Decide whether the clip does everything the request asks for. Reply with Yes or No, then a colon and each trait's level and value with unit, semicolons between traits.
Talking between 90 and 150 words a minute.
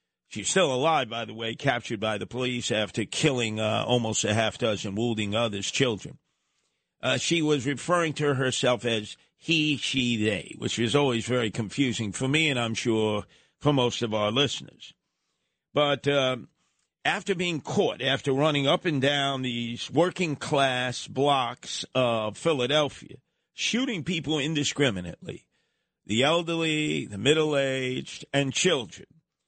Yes: average, 145 wpm